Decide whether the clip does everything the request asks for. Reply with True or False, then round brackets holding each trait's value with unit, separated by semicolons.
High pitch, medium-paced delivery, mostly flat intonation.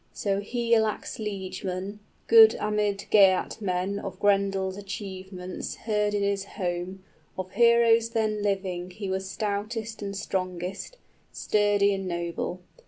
False (200 Hz; 115 wpm; 2.0 semitones)